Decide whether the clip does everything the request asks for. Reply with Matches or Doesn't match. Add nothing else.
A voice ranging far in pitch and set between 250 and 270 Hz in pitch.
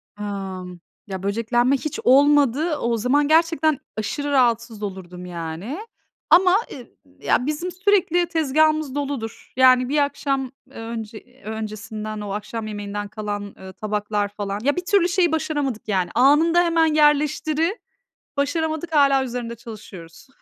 Matches